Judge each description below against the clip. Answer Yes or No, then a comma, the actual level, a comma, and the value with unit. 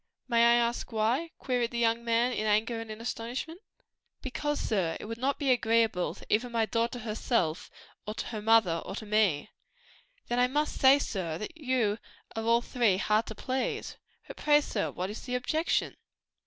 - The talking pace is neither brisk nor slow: Yes, average, 180 wpm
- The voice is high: Yes, high, 230 Hz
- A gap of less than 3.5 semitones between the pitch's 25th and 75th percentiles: Yes, narrow, 2.6 semitones